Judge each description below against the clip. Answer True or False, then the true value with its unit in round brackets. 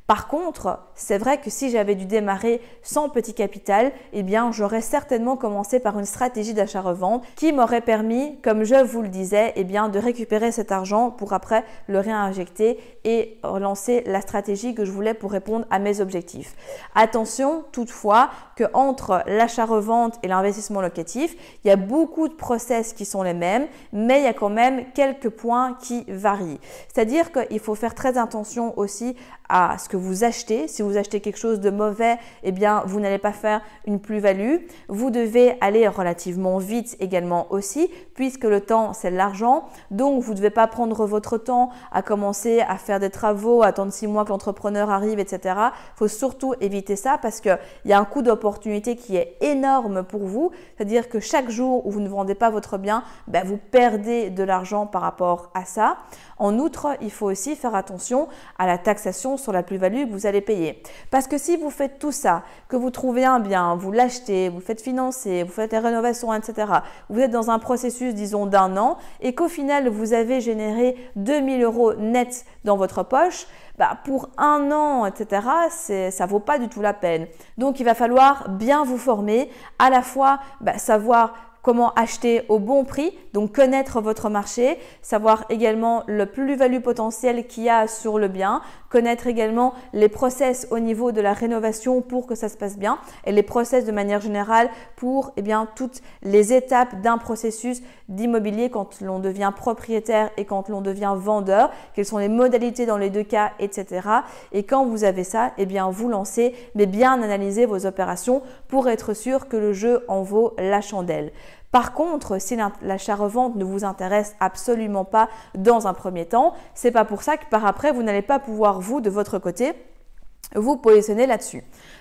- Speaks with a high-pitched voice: True (225 Hz)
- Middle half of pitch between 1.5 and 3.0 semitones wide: False (3.5 semitones)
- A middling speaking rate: True (190 wpm)